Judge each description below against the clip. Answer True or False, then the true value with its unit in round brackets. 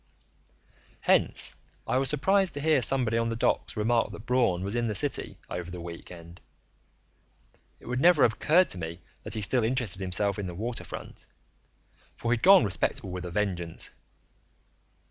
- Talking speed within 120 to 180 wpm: True (170 wpm)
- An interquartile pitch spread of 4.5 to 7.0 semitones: True (5.6 semitones)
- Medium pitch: False (110 Hz)